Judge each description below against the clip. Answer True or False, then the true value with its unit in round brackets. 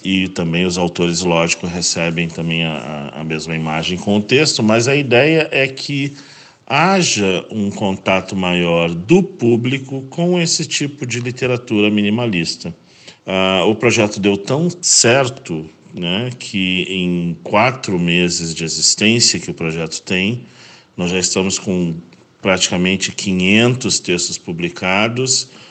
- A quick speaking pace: False (130 wpm)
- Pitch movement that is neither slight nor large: False (6.3 semitones)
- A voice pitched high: False (95 Hz)